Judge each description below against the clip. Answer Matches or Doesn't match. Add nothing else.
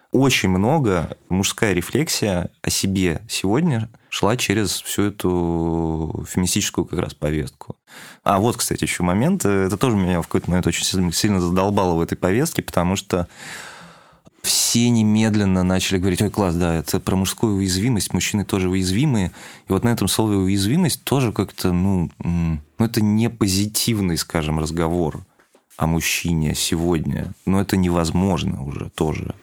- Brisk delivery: Doesn't match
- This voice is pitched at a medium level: Doesn't match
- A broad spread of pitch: Doesn't match